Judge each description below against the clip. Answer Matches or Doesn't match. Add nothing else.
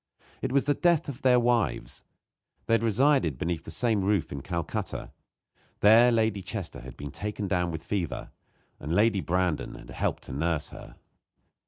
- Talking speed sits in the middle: Matches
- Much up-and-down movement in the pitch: Matches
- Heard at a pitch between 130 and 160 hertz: Doesn't match